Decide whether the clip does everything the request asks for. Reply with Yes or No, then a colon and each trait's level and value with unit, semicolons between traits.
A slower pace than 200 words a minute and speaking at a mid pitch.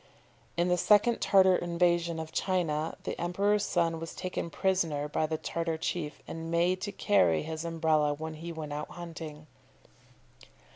Yes: average, 155 wpm; medium, 165 Hz